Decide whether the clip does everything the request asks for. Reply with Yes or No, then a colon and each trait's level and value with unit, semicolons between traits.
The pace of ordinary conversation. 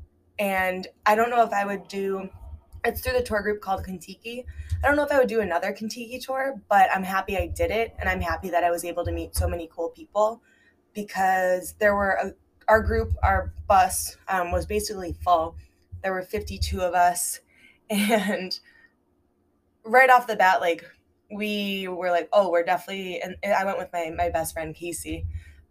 Yes: average, 190 wpm